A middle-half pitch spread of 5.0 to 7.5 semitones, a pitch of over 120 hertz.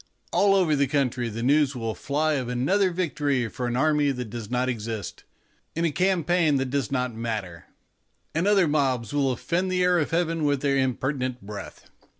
No: average, 4.6 semitones; medium, 140 Hz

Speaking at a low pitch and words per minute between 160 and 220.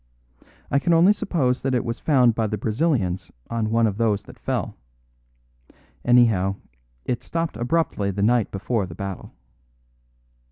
No: low, 115 Hz; average, 150 wpm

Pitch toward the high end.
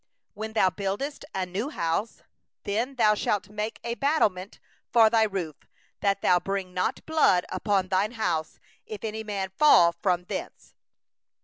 Yes: high, 205 Hz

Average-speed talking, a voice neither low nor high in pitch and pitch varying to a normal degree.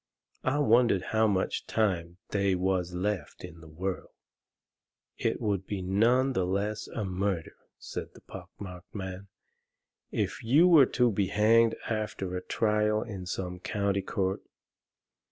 No: average, 145 wpm; low, 100 Hz; average, 3.0 semitones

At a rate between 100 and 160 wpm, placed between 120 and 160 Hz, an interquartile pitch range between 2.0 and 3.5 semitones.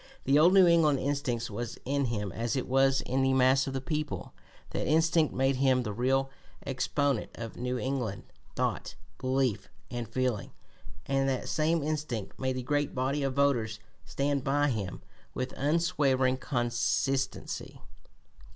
Yes: average, 150 wpm; low, 135 Hz; narrow, 2.4 semitones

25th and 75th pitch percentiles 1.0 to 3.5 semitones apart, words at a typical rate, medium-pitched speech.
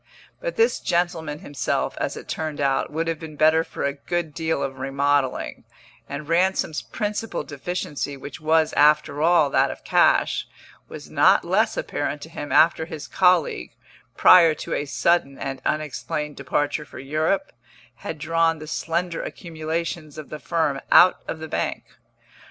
Yes: narrow, 2.6 semitones; average, 155 wpm; medium, 155 Hz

